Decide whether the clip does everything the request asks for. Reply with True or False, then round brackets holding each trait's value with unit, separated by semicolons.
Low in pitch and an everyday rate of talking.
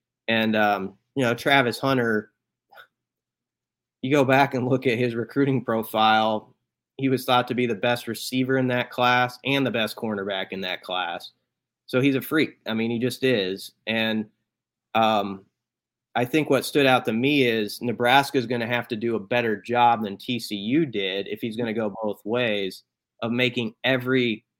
True (120 Hz; 185 wpm)